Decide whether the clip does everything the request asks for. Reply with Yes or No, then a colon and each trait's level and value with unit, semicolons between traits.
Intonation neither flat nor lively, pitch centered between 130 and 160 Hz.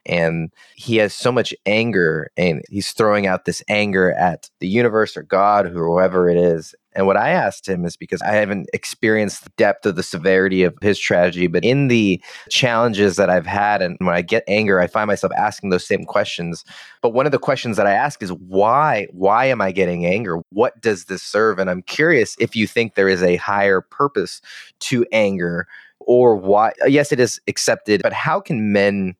No: average, 3.0 semitones; low, 100 Hz